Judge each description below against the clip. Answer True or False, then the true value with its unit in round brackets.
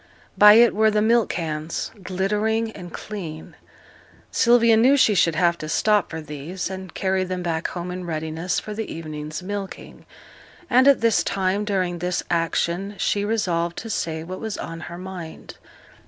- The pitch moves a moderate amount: True (4.1 semitones)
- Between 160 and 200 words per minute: True (170 wpm)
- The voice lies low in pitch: False (185 Hz)